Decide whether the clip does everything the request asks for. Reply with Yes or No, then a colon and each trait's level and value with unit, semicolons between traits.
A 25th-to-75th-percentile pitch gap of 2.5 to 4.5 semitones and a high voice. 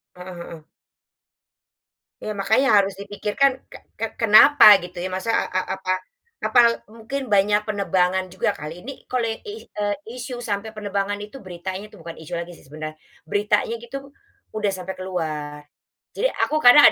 Yes: average, 3.8 semitones; high, 200 Hz